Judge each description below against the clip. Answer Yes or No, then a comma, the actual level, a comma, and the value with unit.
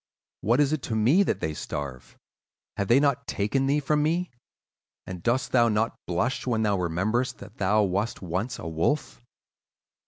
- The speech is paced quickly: No, average, 175 wpm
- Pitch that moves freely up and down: Yes, wide, 6.3 semitones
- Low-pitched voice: Yes, low, 110 Hz